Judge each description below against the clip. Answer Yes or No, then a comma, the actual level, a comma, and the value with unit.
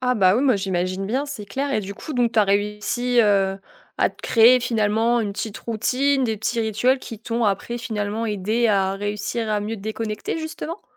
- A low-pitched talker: No, high, 220 Hz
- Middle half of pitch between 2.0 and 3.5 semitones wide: Yes, average, 3.0 semitones